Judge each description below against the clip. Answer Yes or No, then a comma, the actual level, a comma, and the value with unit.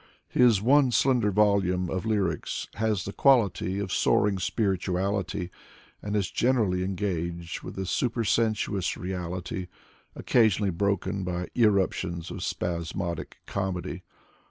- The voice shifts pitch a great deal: No, average, 2.8 semitones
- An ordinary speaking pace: No, slow, 110 wpm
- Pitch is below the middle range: Yes, very low, 95 Hz